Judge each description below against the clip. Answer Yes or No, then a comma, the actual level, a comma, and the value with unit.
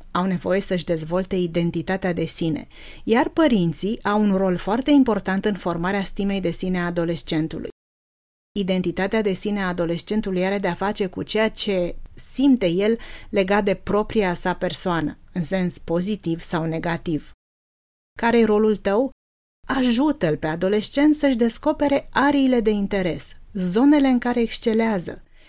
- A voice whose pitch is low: No, high, 190 Hz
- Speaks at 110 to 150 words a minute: Yes, average, 140 wpm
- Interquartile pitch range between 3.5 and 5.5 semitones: Yes, average, 4.0 semitones